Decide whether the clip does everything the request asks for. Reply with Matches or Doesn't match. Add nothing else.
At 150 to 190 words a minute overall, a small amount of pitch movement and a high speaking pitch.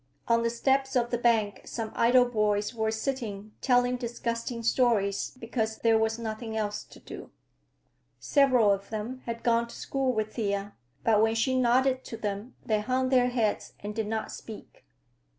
Matches